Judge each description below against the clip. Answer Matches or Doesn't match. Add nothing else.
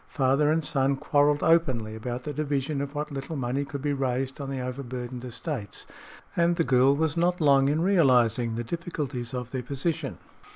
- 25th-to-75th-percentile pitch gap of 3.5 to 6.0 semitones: Doesn't match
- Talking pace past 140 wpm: Matches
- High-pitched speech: Doesn't match